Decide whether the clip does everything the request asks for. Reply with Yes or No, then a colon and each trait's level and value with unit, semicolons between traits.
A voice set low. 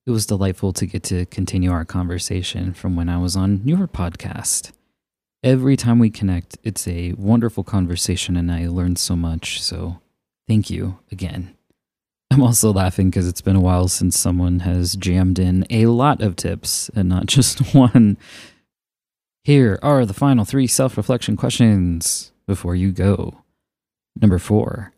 Yes: very low, 95 Hz